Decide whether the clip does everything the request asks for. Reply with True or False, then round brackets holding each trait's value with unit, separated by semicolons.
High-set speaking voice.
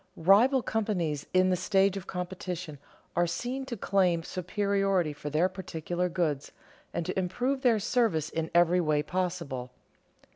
False (180 Hz)